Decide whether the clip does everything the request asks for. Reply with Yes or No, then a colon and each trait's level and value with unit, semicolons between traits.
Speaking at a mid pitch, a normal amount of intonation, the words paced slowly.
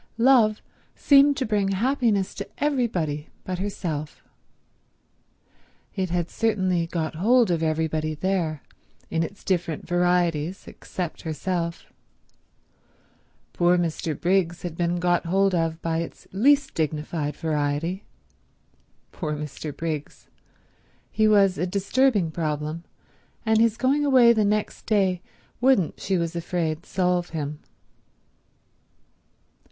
Yes: medium, 175 Hz; average, 4.2 semitones; slow, 115 wpm